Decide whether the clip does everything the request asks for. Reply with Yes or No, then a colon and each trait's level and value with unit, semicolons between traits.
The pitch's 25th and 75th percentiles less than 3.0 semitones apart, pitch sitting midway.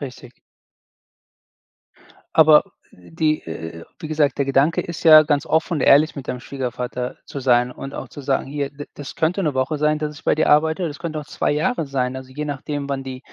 Yes: narrow, 2.5 semitones; medium, 145 Hz